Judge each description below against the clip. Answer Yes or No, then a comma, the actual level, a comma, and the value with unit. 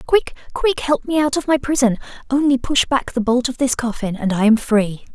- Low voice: No, very high, 255 Hz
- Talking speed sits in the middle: No, fast, 235 wpm